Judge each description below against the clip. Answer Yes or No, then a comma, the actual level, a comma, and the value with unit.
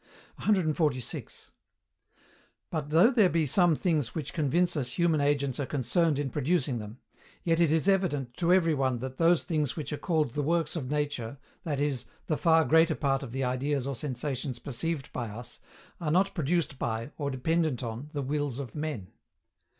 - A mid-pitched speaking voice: Yes, medium, 145 Hz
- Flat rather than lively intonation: No, average, 4.0 semitones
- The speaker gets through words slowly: No, average, 180 wpm